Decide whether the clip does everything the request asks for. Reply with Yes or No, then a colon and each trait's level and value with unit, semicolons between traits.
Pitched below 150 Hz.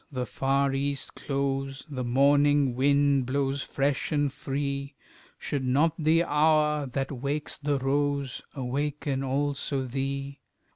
Yes: medium, 140 Hz